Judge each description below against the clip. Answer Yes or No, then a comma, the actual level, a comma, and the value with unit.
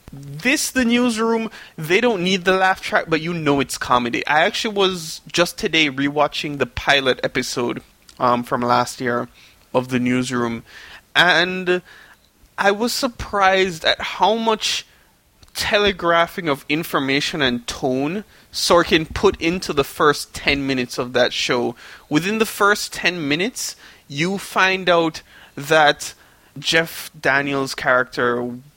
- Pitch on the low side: No, medium, 160 Hz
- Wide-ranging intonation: Yes, wide, 5.9 semitones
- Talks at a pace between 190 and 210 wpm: No, slow, 135 wpm